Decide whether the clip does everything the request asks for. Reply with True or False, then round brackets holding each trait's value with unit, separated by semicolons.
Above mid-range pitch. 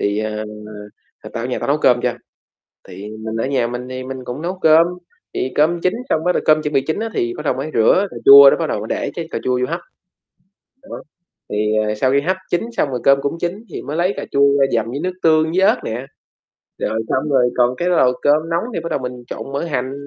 False (140 Hz)